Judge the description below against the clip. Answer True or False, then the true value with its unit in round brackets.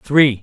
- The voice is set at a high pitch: False (130 Hz)